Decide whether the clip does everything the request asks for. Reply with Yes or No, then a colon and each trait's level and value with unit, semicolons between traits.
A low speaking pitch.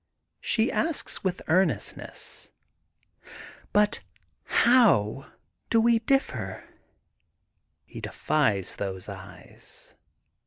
No: high, 190 Hz